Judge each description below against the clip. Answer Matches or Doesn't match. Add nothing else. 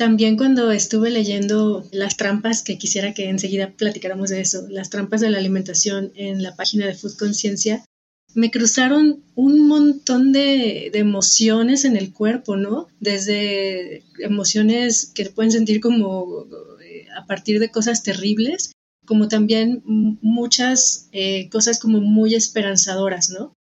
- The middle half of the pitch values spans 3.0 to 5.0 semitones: Doesn't match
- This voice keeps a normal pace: Matches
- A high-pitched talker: Matches